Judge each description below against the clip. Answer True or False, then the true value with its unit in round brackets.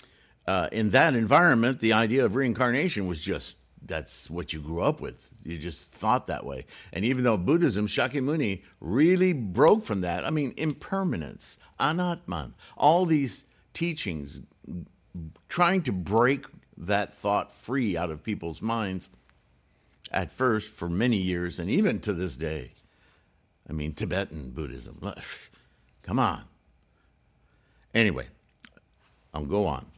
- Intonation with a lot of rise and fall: True (7.8 semitones)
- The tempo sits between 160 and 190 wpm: False (135 wpm)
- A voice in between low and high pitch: False (100 Hz)